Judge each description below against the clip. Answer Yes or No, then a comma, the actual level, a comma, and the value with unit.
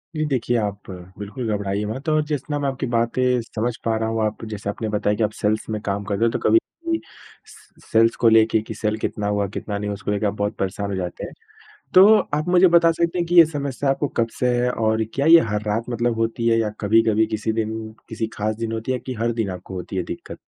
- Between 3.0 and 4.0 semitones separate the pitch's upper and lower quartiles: Yes, average, 3.3 semitones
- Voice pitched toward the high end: No, low, 110 Hz